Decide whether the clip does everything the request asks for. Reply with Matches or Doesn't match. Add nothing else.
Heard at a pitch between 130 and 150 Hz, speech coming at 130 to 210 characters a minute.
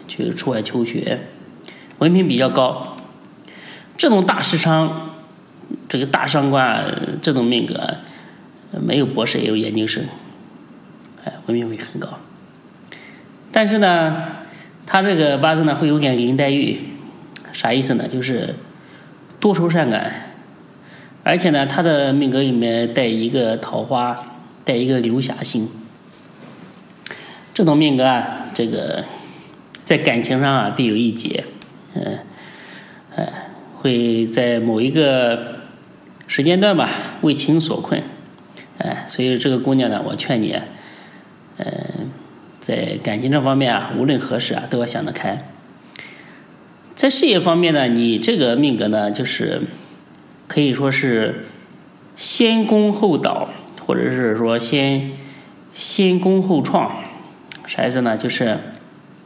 Matches